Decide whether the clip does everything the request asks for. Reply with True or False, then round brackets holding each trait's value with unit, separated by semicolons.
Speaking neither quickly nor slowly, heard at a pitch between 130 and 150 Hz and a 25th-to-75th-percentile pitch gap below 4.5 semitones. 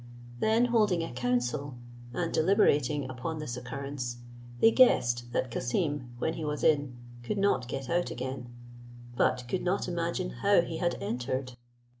False (150 wpm; 140 Hz; 5.3 semitones)